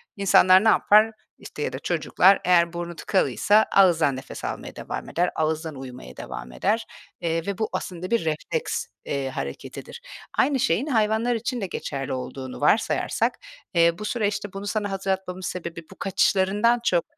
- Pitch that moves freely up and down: No, average, 4.3 semitones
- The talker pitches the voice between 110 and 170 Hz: No, medium, 185 Hz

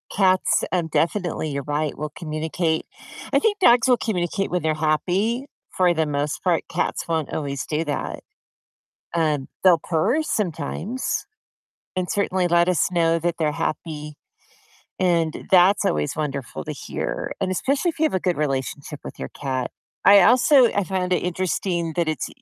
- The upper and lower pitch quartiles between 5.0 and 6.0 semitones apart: No, average, 3.6 semitones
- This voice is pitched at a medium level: Yes, medium, 170 Hz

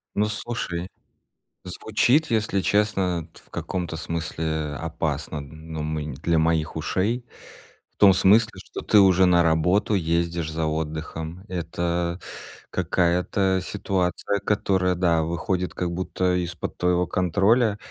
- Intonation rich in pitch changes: No, average, 3.0 semitones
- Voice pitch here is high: No, very low, 90 Hz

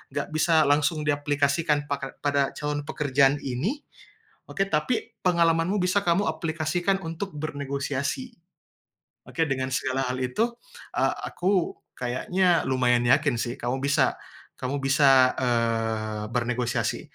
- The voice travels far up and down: No, average, 4.1 semitones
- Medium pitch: Yes, medium, 145 Hz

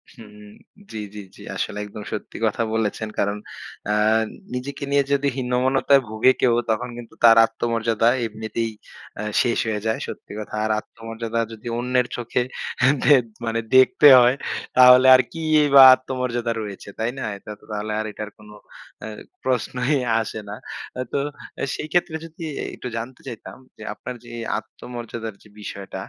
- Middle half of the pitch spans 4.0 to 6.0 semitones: No, narrow, 2.6 semitones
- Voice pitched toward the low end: Yes, low, 115 Hz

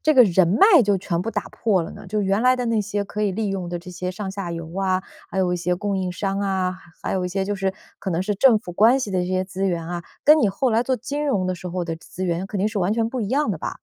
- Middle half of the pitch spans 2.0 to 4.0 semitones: Yes, average, 3.0 semitones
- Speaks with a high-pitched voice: Yes, high, 195 Hz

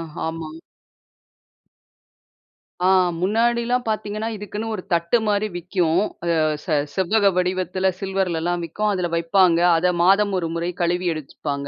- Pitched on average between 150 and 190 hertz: Yes, medium, 185 Hz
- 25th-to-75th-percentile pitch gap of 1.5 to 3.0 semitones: No, average, 3.5 semitones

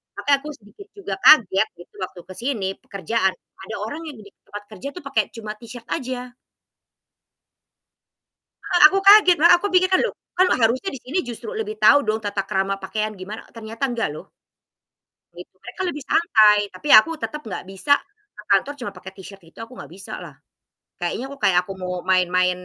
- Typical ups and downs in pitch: No, wide, 7.1 semitones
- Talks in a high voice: Yes, high, 225 Hz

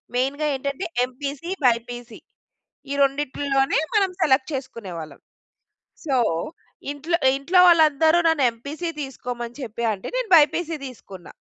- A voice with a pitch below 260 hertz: No, very high, 275 Hz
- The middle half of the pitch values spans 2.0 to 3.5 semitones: No, average, 4.2 semitones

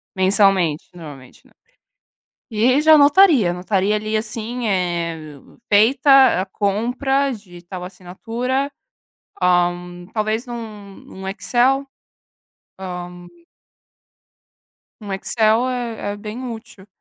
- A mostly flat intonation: No, average, 5.1 semitones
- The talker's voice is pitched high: Yes, high, 210 Hz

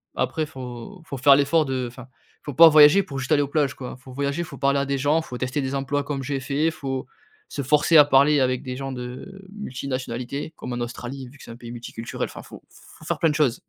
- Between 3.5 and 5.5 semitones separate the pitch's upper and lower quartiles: No, narrow, 2.5 semitones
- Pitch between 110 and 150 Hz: Yes, medium, 140 Hz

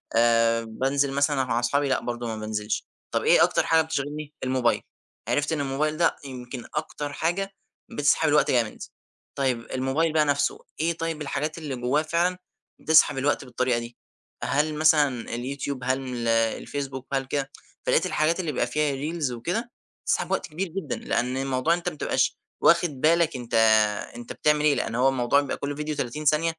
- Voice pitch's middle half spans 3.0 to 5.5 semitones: Yes, average, 3.5 semitones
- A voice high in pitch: No, medium, 140 Hz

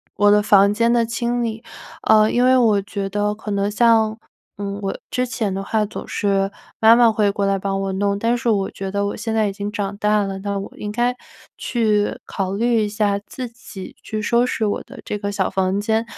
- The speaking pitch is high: Yes, high, 210 Hz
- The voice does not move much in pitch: Yes, narrow, 2.3 semitones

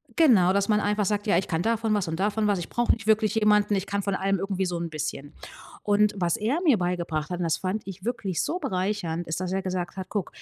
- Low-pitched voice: No, high, 195 Hz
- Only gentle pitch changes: No, average, 3.1 semitones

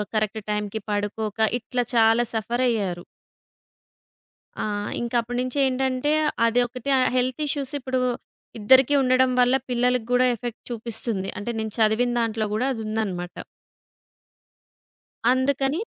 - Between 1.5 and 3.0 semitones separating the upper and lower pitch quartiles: Yes, average, 2.7 semitones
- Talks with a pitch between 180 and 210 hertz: No, high, 240 Hz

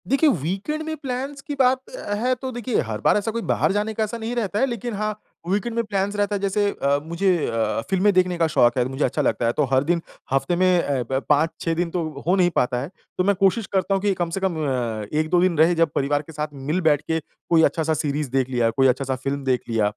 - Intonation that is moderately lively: No, wide, 6.7 semitones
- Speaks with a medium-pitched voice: Yes, medium, 175 Hz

